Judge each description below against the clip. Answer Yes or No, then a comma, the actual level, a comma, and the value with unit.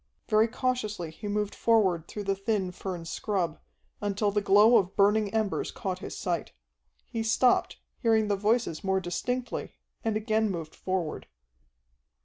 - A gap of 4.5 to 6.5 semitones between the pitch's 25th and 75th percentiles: No, average, 2.7 semitones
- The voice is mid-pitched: No, high, 205 Hz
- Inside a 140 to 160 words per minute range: Yes, average, 145 wpm